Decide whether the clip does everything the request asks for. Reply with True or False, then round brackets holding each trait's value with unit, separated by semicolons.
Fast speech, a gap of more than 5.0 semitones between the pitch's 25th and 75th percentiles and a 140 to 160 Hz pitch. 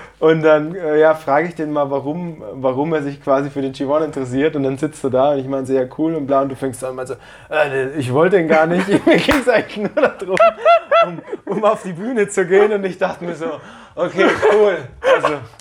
True (240 wpm; 5.5 semitones; 155 Hz)